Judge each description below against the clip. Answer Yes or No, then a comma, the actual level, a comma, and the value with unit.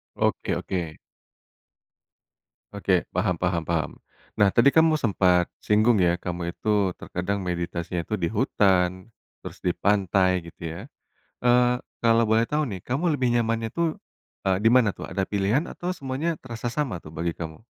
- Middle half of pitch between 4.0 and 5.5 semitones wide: Yes, average, 4.9 semitones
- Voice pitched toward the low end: Yes, low, 100 Hz